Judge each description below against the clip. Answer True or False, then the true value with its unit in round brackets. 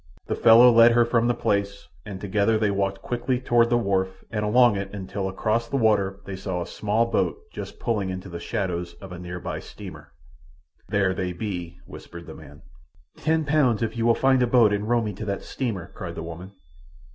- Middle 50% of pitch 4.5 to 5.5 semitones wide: False (3.8 semitones)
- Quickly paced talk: True (210 wpm)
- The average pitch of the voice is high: False (105 Hz)